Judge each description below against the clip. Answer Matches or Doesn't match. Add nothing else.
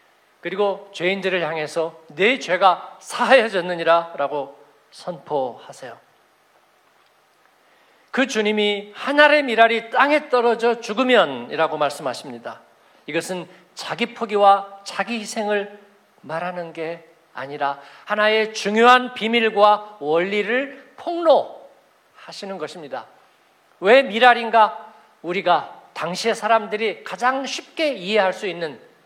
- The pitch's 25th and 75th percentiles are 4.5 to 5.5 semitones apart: Matches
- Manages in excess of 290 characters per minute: Doesn't match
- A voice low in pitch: Doesn't match